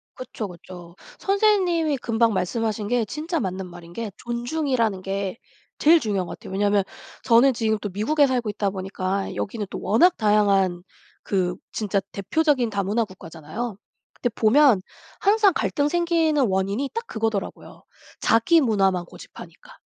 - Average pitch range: No, wide, 6.5 semitones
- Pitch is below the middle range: No, high, 220 Hz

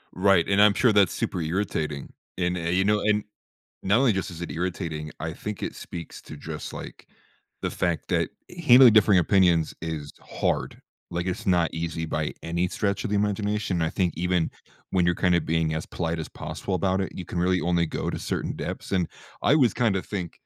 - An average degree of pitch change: Yes, average, 3.3 semitones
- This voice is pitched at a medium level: No, very low, 90 Hz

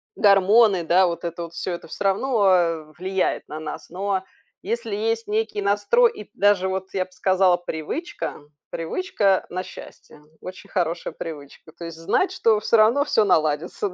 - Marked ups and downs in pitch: No, average, 3.7 semitones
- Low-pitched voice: No, high, 190 Hz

